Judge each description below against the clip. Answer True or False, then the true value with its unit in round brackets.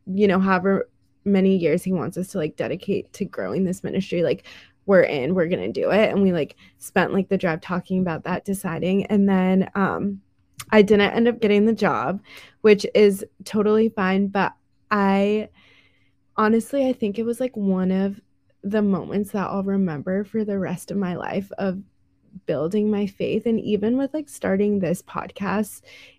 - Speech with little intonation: True (2.2 semitones)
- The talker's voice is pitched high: True (195 Hz)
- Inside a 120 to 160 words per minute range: False (180 wpm)